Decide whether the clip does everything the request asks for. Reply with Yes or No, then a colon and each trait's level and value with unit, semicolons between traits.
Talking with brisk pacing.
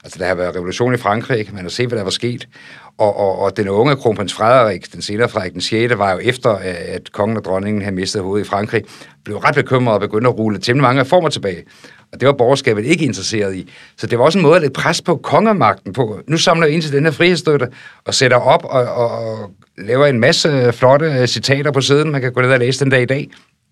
Yes: fast, 250 wpm